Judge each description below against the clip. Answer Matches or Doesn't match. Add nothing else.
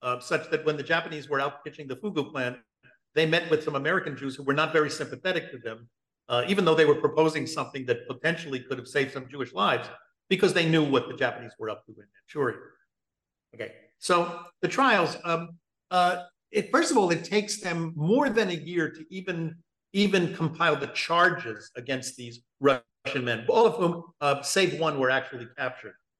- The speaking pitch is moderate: Matches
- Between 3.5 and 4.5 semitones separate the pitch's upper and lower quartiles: Matches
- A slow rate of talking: Doesn't match